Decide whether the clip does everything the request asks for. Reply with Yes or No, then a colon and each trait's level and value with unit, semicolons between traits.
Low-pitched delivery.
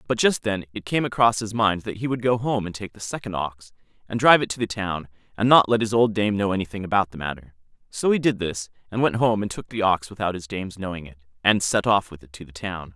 Yes: low, 100 Hz